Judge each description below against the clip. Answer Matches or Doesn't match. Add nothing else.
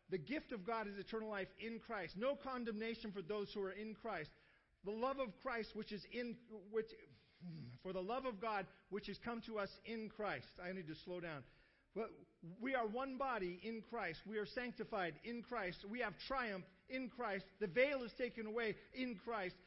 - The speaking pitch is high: Matches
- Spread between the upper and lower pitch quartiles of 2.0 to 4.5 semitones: Matches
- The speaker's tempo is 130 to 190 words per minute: Doesn't match